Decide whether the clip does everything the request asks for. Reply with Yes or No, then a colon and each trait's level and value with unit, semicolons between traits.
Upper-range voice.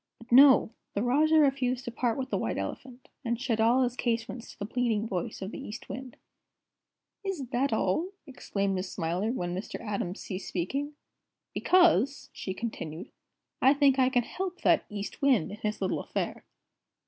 Yes: high, 240 Hz